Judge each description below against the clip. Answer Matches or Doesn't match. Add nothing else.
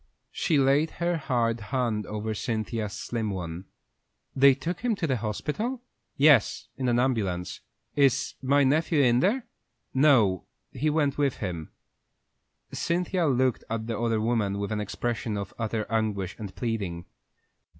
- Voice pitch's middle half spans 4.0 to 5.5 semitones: Matches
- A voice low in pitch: Matches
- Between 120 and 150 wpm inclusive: Matches